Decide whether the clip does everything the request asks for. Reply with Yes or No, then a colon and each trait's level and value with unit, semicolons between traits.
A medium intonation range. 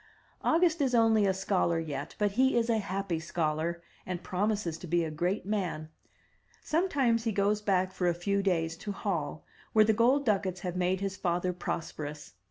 Yes: average, 4.0 semitones